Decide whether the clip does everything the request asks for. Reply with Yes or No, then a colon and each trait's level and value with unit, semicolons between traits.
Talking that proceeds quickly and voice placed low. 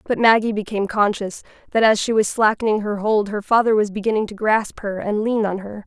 No: fast, 225 wpm; high, 210 Hz